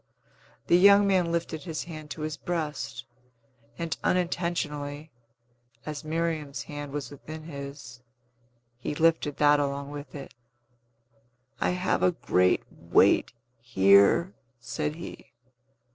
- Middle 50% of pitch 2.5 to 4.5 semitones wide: Yes, average, 2.9 semitones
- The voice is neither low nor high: Yes, medium, 150 Hz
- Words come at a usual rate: No, slow, 115 wpm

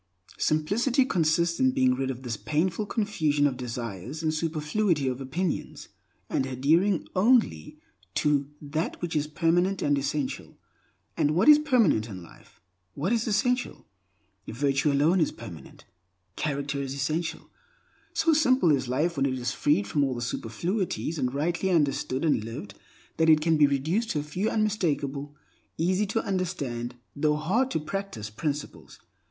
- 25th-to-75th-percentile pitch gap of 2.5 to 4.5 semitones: No, average, 5.3 semitones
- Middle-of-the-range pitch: Yes, medium, 155 Hz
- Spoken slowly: No, average, 150 wpm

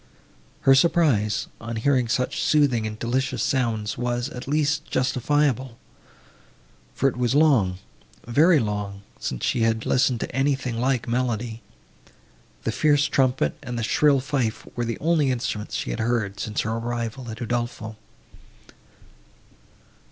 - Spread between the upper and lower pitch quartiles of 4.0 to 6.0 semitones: No, average, 3.3 semitones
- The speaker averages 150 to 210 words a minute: No, slow, 135 wpm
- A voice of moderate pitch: No, low, 120 Hz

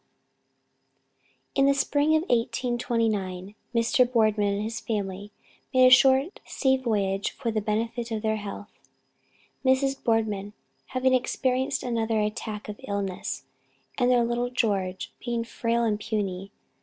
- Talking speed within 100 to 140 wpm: Yes, slow, 135 wpm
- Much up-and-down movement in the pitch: No, average, 3.3 semitones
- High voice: Yes, high, 230 Hz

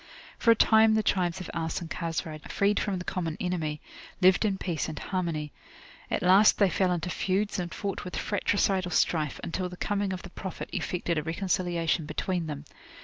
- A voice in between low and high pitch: Yes, medium, 180 Hz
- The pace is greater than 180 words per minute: Yes, average, 190 wpm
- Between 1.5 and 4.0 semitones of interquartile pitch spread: Yes, average, 2.8 semitones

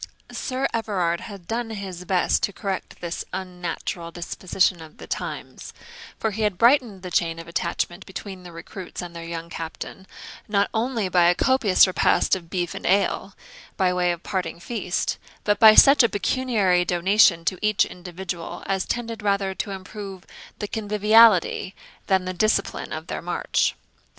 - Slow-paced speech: No, average, 165 wpm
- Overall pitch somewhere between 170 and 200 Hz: Yes, high, 190 Hz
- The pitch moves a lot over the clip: No, average, 3.2 semitones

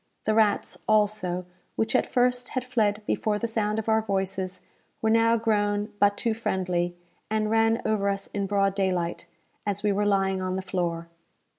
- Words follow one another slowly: No, average, 175 wpm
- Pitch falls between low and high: No, high, 205 Hz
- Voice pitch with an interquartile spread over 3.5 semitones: No, narrow, 2.4 semitones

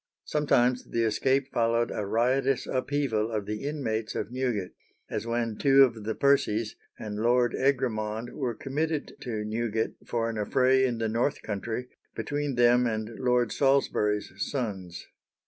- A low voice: Yes, low, 120 Hz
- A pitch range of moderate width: Yes, average, 3.3 semitones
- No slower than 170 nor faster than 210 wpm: No, average, 145 wpm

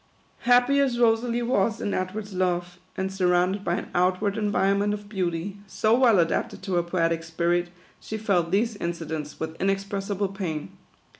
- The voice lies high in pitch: Yes, high, 195 Hz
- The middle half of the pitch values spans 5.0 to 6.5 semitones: No, average, 3.2 semitones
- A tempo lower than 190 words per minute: Yes, average, 160 wpm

